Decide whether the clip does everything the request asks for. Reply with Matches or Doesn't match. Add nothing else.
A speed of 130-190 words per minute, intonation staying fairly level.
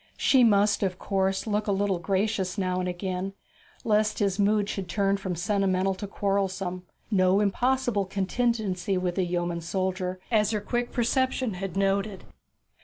Matches